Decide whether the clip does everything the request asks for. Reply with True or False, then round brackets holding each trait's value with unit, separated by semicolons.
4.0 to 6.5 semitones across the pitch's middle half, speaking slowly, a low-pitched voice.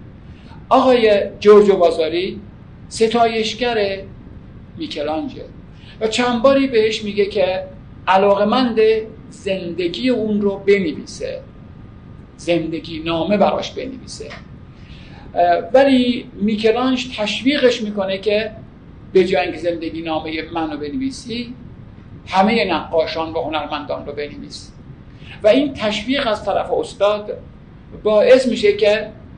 False (5.0 semitones; 95 wpm; 205 Hz)